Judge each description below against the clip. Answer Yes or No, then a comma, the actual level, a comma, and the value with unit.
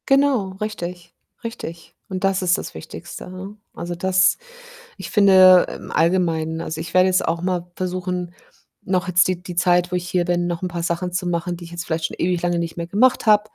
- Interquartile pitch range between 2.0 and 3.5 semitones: No, narrow, 1.5 semitones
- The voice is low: No, medium, 180 Hz